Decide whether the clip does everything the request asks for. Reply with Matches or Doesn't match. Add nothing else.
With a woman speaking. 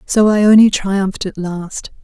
Matches